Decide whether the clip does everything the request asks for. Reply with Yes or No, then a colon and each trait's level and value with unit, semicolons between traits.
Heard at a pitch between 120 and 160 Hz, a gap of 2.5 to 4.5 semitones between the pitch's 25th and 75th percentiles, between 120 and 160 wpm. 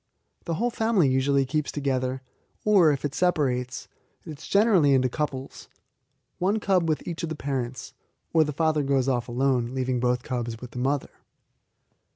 No: medium, 140 Hz; average, 3.9 semitones; average, 170 wpm